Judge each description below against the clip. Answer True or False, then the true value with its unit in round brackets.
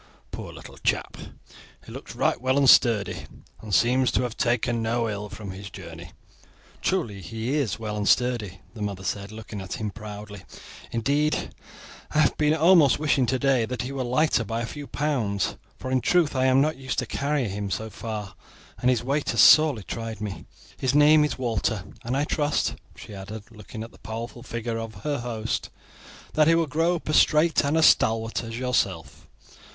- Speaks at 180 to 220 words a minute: True (190 wpm)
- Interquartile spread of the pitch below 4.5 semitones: False (4.8 semitones)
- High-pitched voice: False (120 Hz)